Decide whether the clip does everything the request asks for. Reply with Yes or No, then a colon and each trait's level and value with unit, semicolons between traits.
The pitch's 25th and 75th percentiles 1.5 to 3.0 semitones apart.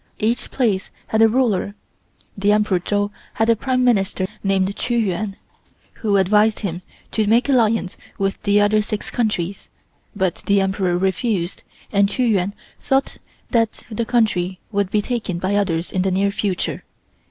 Yes: average, 2.7 semitones